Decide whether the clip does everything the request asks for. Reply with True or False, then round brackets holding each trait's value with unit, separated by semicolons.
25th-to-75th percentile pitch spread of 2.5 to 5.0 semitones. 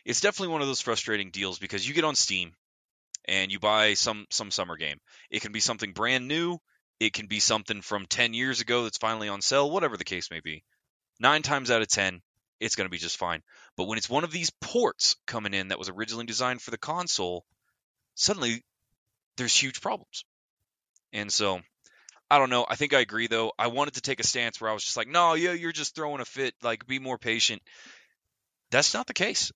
True (4.3 semitones)